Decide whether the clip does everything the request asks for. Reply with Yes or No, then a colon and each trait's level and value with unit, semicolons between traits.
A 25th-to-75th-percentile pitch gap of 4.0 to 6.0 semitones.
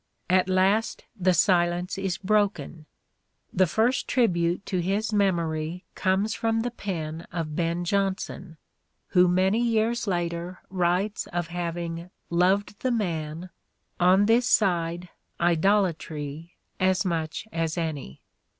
No: average, 2.9 semitones